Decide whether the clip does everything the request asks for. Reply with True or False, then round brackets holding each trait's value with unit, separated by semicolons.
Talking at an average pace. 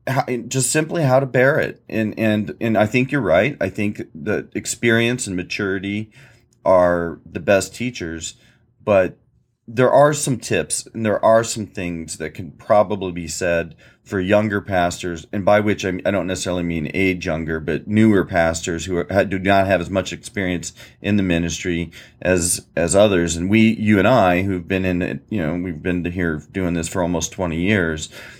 True (190 wpm)